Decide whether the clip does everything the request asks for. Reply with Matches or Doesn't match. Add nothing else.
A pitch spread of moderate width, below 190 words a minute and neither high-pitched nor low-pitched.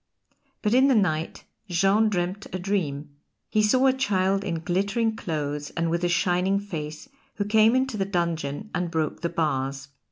Matches